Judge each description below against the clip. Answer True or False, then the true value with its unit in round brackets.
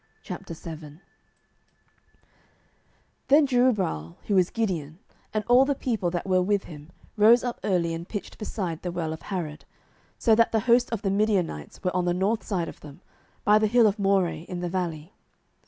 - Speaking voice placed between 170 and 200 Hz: True (190 Hz)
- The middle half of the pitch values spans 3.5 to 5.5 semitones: True (4.5 semitones)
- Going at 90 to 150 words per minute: False (175 wpm)